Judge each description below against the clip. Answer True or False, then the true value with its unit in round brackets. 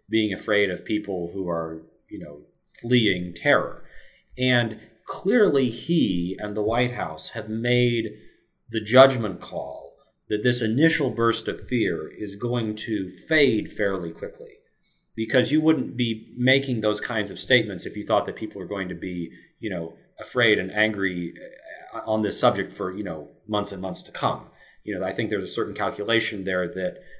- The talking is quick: False (170 wpm)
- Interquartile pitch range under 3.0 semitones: False (4.0 semitones)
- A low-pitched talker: True (110 Hz)